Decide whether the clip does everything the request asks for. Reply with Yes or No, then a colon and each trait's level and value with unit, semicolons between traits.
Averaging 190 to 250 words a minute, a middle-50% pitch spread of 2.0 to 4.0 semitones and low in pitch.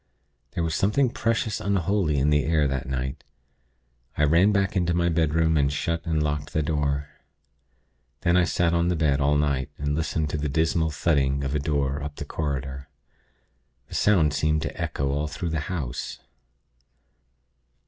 No: average, 170 wpm; average, 2.8 semitones; very low, 75 Hz